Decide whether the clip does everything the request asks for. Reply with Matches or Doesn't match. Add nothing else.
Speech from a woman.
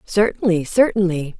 Matches